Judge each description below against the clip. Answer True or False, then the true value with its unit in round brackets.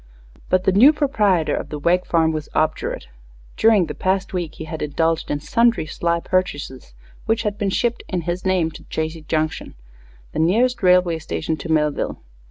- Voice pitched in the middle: True (170 Hz)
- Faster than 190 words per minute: False (180 wpm)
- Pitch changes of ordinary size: True (3.6 semitones)